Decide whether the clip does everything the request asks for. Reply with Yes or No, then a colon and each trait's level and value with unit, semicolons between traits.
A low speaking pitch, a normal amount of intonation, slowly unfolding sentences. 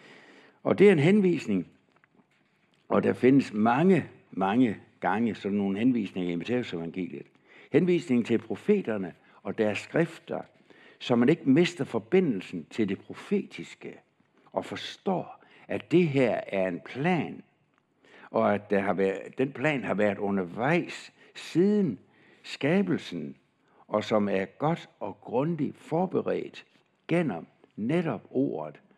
No: low, 120 Hz; wide, 9.0 semitones; slow, 125 wpm